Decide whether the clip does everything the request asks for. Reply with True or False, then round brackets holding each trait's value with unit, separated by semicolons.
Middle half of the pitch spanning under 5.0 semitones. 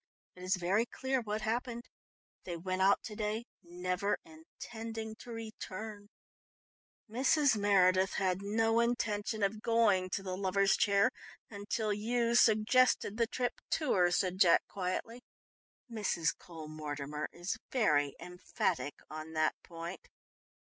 True (3.8 semitones)